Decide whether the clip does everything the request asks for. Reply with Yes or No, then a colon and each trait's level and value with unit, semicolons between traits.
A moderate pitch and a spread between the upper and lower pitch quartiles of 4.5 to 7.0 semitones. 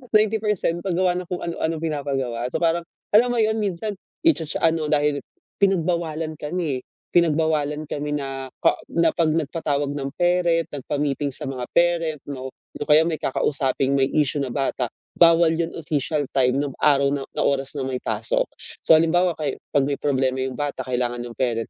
No: medium, 150 Hz; average, 3.6 semitones